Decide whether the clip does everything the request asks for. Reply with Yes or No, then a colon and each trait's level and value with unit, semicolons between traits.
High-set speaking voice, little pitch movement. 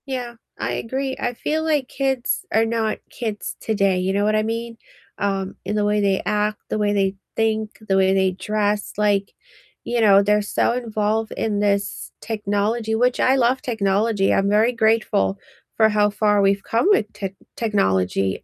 Yes: high, 210 Hz; narrow, 2.3 semitones